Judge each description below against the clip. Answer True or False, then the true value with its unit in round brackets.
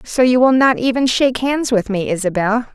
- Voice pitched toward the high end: True (240 Hz)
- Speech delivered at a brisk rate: True (220 wpm)